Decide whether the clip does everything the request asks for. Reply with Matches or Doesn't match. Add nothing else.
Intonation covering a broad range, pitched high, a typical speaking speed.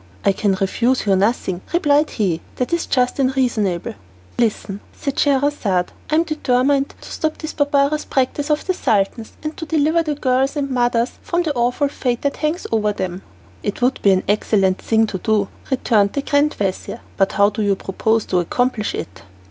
Matches